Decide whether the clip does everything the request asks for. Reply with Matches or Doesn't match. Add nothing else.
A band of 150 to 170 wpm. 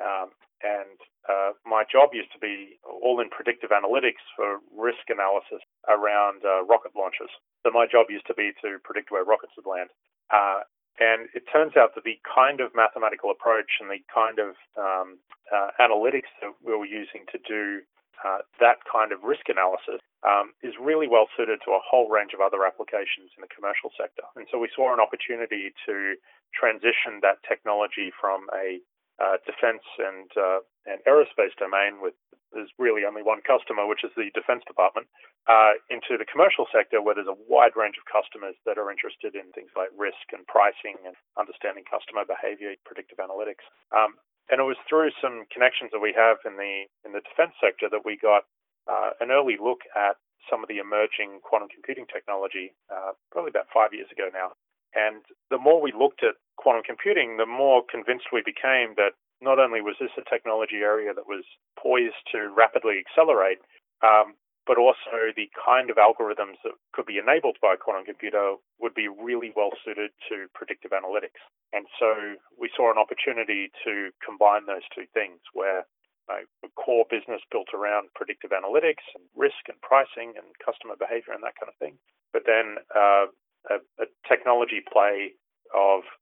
Doesn't match